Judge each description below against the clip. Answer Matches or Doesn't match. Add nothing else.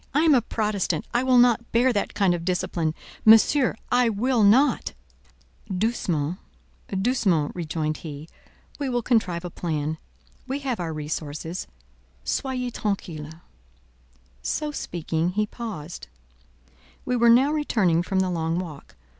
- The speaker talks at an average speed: Doesn't match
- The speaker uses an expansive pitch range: Matches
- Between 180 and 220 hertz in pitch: Matches